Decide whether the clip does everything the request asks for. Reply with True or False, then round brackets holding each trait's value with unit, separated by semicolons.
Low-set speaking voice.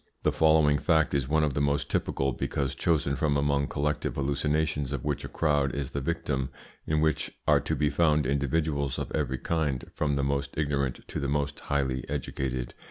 True (70 Hz)